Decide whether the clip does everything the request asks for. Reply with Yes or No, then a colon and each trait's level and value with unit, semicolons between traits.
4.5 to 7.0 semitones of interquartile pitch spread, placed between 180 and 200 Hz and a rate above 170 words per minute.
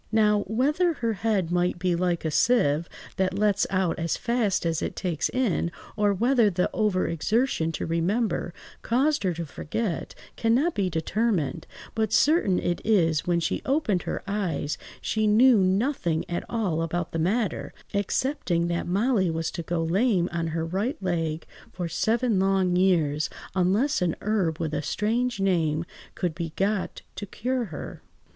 No: average, 4.9 semitones; high, 190 Hz; average, 160 wpm